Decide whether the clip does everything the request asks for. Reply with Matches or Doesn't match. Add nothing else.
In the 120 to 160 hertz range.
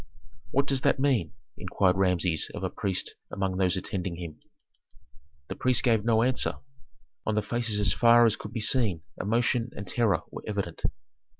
Doesn't match